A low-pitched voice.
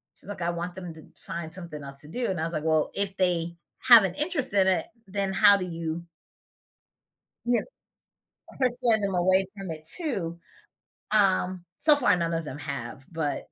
No: medium, 180 Hz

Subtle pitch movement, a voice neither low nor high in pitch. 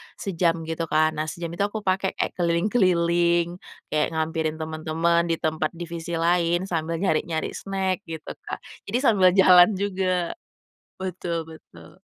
Yes: narrow, 2.3 semitones; medium, 170 Hz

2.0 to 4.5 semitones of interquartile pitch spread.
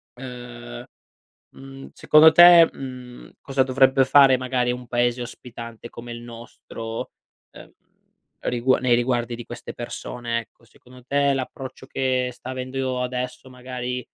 No: narrow, 1.5 semitones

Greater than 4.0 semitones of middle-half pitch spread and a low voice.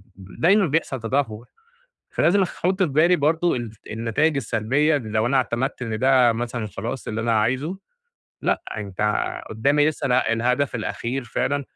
Yes: average, 4.6 semitones; low, 125 Hz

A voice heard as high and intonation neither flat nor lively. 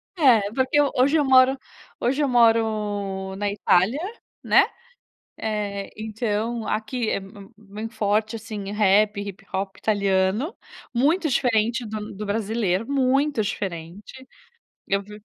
Yes: high, 215 Hz; average, 3.3 semitones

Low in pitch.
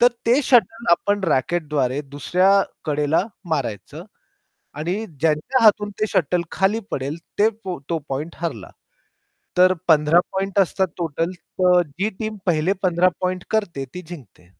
No: medium, 175 Hz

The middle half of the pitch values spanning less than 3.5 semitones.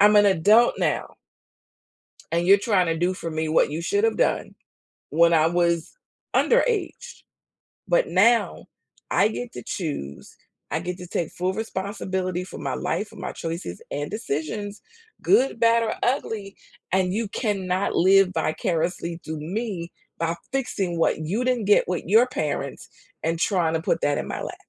No: average, 4.7 semitones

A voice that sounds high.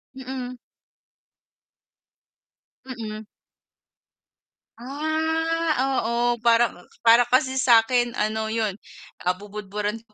Yes: high, 235 Hz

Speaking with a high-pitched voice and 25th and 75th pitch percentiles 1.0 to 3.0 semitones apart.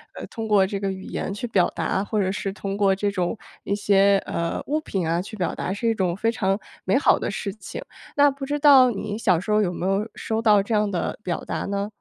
Yes: high, 200 Hz; narrow, 2.4 semitones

